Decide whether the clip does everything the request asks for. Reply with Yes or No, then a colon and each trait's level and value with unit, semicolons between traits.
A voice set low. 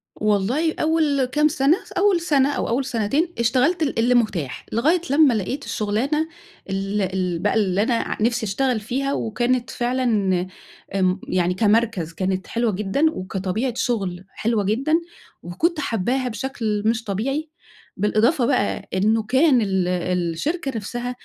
No: high, 230 Hz